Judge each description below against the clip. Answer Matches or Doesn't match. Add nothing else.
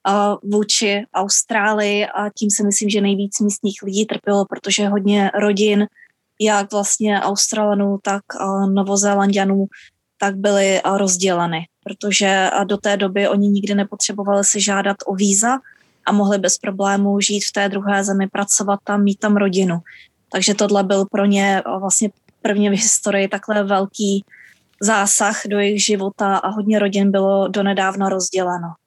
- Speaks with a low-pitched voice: Doesn't match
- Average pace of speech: Matches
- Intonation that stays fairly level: Matches